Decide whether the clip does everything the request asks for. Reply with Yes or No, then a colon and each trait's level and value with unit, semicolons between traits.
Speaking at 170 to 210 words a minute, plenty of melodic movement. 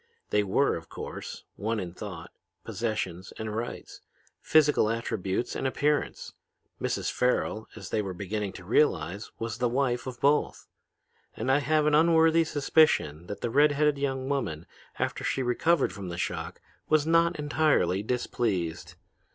No: average, 150 wpm; wide, 6.7 semitones